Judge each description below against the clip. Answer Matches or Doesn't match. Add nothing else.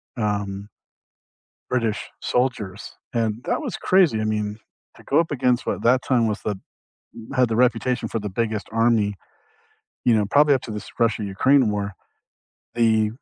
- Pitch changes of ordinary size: Matches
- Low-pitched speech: Matches